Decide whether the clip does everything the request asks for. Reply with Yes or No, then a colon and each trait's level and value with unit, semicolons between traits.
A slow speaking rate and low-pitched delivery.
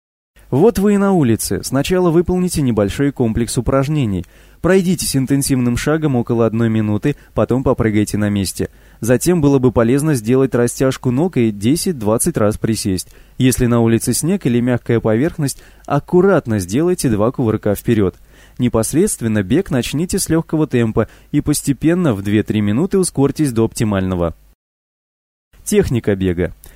No: average, 130 wpm; low, 120 Hz